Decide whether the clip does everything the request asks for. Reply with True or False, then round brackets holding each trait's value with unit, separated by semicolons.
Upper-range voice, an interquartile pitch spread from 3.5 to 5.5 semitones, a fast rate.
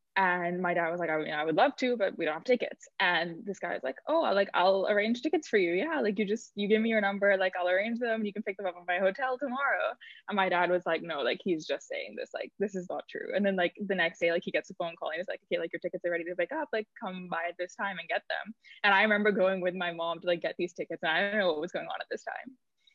True (195 Hz; 4.0 semitones; 320 wpm)